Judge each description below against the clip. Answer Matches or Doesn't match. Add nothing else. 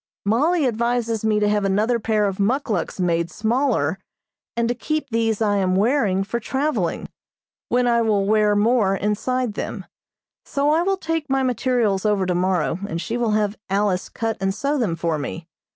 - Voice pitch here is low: Doesn't match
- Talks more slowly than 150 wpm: Doesn't match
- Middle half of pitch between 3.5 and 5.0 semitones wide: Matches